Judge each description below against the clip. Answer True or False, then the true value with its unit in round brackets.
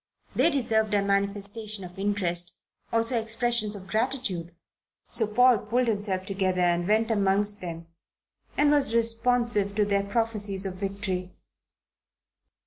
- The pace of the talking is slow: True (130 wpm)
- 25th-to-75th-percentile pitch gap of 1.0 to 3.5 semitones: True (2.9 semitones)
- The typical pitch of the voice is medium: False (205 Hz)